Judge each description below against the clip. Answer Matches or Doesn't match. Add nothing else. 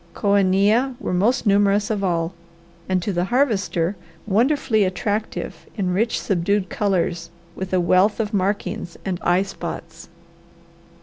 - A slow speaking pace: Matches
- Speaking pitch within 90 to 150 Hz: Doesn't match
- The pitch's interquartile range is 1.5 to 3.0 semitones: Matches